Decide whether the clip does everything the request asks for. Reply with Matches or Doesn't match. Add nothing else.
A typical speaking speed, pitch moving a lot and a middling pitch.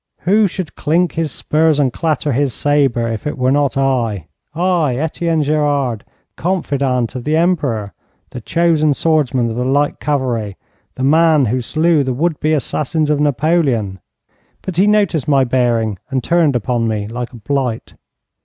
Doesn't match